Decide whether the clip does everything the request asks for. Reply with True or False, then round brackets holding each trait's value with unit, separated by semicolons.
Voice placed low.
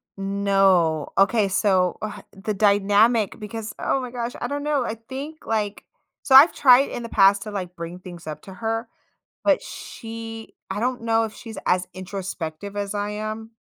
False (210 Hz)